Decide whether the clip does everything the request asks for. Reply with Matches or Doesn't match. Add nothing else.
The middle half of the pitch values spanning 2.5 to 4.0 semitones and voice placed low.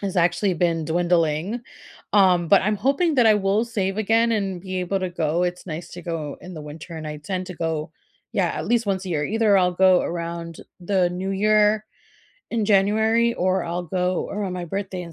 Doesn't match